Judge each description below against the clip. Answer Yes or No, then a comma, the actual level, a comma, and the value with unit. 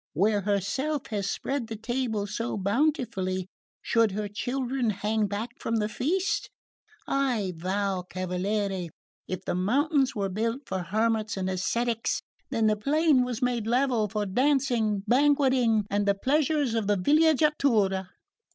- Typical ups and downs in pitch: Yes, average, 4.6 semitones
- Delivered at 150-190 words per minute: No, average, 140 wpm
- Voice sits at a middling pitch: No, high, 220 Hz